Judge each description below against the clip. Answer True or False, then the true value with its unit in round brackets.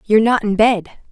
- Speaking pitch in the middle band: False (215 Hz)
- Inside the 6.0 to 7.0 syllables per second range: True (6.2 syllables/s)